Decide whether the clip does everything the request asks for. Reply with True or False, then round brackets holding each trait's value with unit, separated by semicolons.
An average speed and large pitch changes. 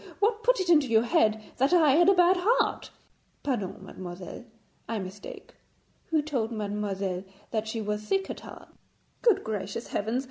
True (165 wpm; 8.9 semitones)